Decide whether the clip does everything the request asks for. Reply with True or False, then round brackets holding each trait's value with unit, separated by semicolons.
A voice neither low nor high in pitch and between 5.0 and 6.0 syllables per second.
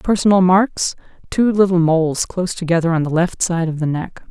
True (175 Hz; 5.5 syllables/s)